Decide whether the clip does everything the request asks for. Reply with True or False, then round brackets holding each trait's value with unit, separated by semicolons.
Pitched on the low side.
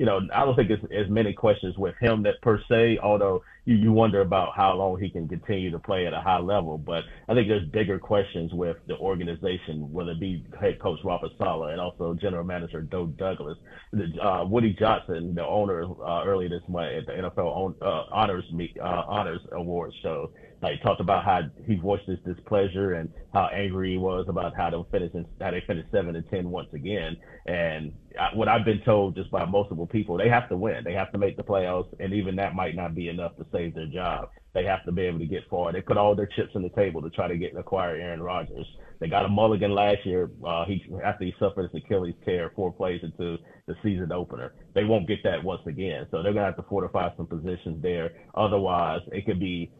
True (95 Hz)